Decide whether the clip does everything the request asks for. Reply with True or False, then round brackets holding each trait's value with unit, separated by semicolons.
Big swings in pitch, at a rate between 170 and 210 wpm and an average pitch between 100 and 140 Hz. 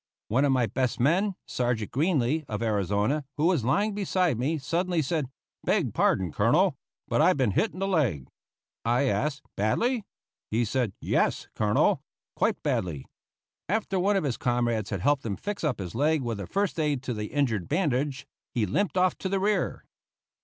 True (7.6 semitones; 180 wpm; 135 Hz)